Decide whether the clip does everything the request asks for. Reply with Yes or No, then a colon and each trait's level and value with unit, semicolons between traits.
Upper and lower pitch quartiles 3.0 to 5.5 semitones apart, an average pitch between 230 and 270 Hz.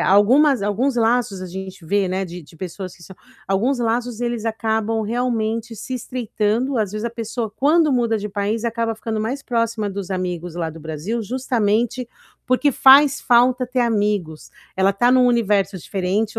No: average, 3.7 semitones; high, 220 Hz